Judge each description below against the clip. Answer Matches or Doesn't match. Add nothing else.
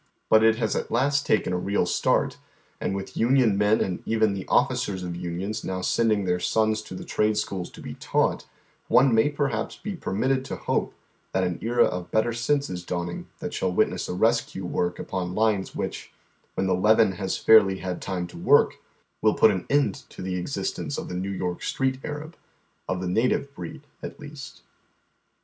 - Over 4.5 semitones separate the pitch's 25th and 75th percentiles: Doesn't match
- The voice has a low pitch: Matches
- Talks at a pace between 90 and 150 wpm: Doesn't match